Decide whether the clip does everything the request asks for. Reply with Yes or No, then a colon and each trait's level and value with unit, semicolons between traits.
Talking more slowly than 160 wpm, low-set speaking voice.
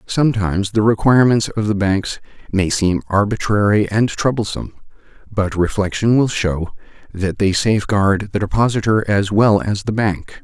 Yes: average, 145 wpm; low, 105 Hz